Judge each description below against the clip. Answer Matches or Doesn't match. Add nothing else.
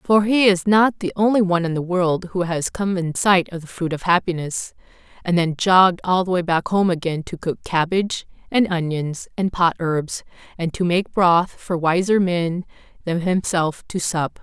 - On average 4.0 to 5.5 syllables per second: Matches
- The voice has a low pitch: Doesn't match